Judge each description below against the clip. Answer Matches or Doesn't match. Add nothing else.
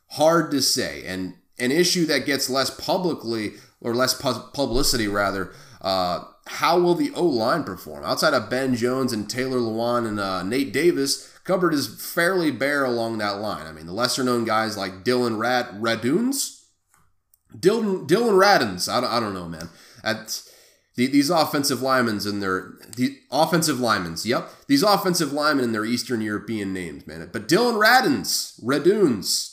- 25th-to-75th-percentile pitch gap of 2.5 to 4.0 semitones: Doesn't match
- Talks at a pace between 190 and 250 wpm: Doesn't match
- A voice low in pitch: Matches